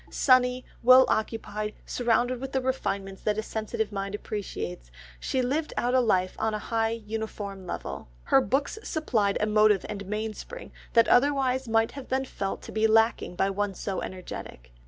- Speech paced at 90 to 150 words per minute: No, average, 170 wpm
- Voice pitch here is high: Yes, high, 220 Hz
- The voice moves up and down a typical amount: Yes, average, 4.0 semitones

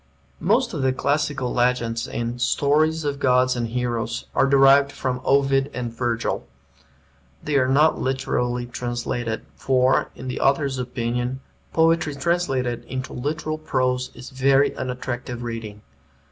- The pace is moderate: No, slow, 130 wpm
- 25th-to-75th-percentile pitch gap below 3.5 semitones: Yes, narrow, 2.4 semitones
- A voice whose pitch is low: Yes, low, 130 Hz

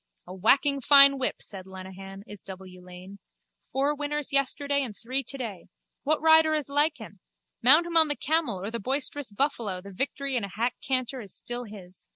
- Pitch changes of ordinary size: No, wide, 6.3 semitones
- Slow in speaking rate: No, average, 190 wpm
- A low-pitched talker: No, very high, 255 Hz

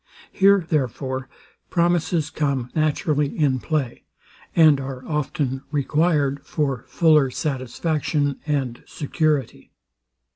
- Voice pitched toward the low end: No, medium, 145 Hz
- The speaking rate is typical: No, slow, 95 wpm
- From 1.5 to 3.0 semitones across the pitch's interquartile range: Yes, average, 2.7 semitones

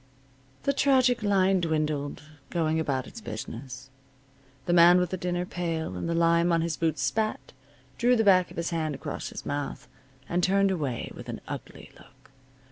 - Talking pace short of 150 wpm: No, average, 175 wpm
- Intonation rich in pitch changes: No, average, 3.7 semitones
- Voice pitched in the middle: Yes, medium, 170 Hz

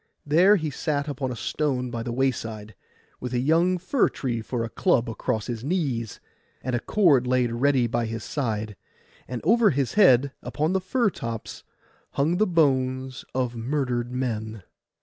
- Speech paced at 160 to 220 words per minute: Yes, average, 170 wpm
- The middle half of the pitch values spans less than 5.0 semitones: Yes, average, 4.4 semitones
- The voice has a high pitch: No, low, 130 Hz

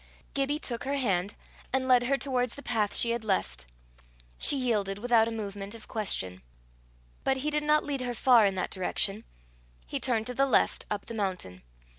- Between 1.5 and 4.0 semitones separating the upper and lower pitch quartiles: No, average, 4.6 semitones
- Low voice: No, high, 230 Hz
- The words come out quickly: No, average, 190 wpm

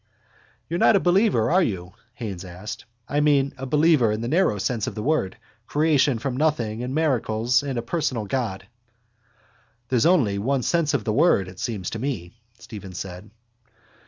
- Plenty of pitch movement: Yes, wide, 5.8 semitones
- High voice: No, low, 120 Hz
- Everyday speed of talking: Yes, average, 175 wpm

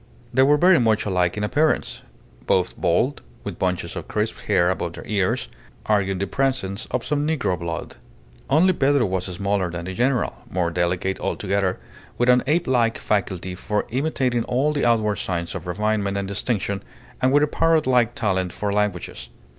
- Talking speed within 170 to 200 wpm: Yes, average, 175 wpm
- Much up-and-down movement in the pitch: Yes, wide, 5.8 semitones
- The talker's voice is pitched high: No, low, 105 Hz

